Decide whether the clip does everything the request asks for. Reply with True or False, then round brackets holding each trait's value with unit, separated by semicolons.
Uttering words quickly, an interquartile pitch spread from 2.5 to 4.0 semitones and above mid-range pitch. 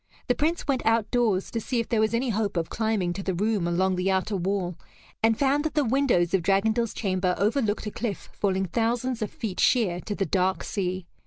True (215 wpm; 3.7 semitones; 210 Hz)